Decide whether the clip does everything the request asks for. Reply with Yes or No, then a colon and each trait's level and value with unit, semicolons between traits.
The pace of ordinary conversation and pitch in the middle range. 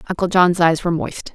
No: fast, 225 wpm; medium, 175 Hz